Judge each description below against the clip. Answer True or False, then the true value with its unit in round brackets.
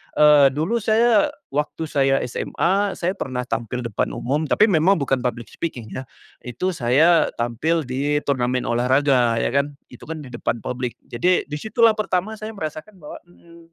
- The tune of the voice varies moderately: False (5.8 semitones)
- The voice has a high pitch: False (145 Hz)